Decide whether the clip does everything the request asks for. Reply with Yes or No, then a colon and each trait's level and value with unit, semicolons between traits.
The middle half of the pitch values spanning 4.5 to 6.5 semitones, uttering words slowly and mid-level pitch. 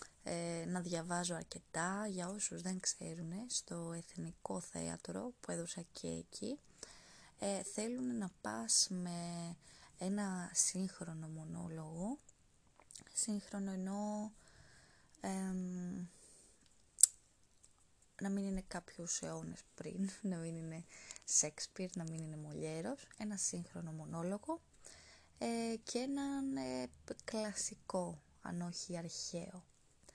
No: average, 3.4 semitones; slow, 100 wpm; medium, 180 Hz